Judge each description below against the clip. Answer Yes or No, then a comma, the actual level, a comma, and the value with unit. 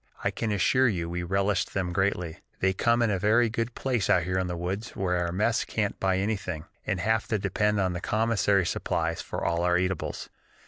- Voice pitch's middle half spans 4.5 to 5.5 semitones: No, average, 3.4 semitones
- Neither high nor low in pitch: No, very low, 95 Hz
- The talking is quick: Yes, fast, 210 wpm